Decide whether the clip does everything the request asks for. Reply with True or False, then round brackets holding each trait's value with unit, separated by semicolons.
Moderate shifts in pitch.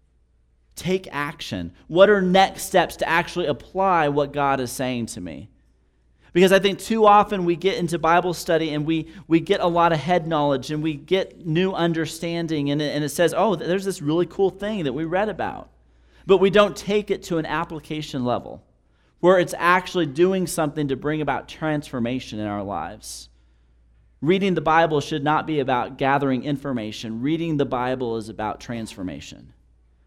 False (6.1 semitones)